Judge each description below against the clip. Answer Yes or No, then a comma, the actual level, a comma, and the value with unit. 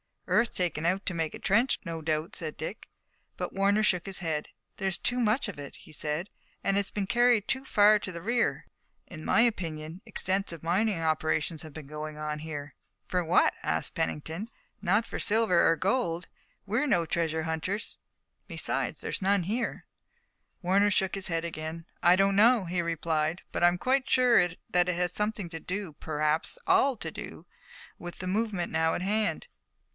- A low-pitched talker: No, medium, 180 Hz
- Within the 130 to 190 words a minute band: Yes, average, 180 wpm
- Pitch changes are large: No, average, 4.3 semitones